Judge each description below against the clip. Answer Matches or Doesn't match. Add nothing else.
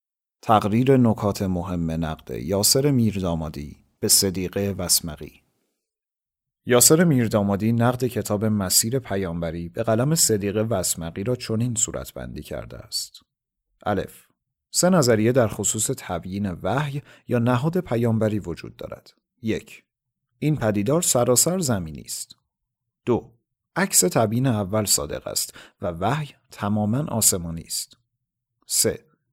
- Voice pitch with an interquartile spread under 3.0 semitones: Doesn't match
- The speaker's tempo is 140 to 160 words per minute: Doesn't match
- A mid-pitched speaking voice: Doesn't match